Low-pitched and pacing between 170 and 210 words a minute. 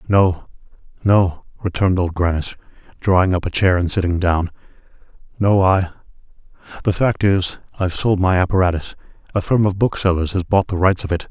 No: very low, 90 Hz; average, 160 wpm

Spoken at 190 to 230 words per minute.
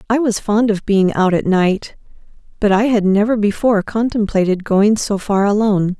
No: average, 180 wpm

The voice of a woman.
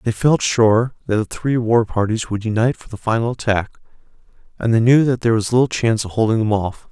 No: male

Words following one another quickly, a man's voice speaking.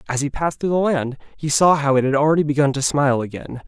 Yes: fast, 260 wpm; male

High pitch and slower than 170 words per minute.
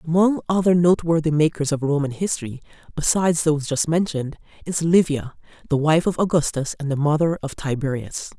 No: medium, 155 Hz; average, 155 wpm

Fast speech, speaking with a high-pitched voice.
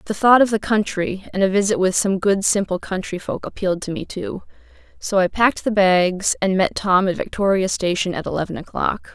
Yes: fast, 210 wpm; high, 195 Hz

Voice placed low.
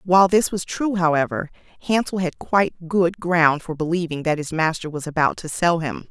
No: medium, 170 Hz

